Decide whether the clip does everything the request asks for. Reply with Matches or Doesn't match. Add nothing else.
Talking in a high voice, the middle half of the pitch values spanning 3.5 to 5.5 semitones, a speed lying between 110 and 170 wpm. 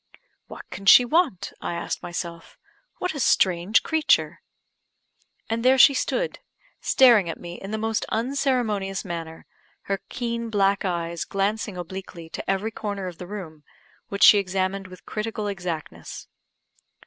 Matches